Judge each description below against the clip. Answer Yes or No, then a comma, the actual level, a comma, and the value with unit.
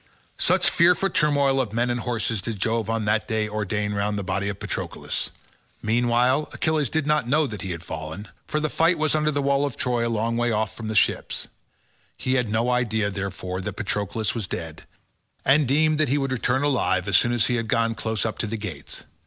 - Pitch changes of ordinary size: Yes, average, 4.6 semitones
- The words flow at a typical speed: No, fast, 215 wpm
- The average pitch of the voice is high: No, low, 115 Hz